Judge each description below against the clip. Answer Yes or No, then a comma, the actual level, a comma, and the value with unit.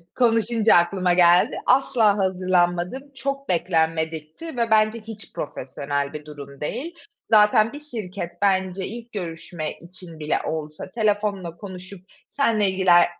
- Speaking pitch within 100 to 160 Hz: No, medium, 185 Hz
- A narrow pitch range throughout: No, average, 4.6 semitones